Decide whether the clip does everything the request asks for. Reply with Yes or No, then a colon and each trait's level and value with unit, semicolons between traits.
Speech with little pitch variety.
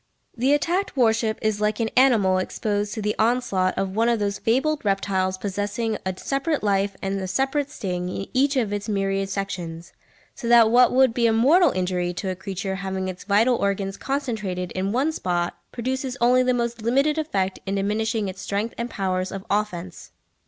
No: average, 4.2 semitones